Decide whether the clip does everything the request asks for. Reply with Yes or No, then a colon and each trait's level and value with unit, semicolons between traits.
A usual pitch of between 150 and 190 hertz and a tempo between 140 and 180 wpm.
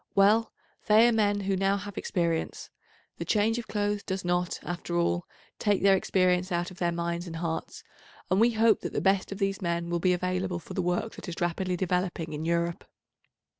No: medium, 185 Hz; fast, 205 wpm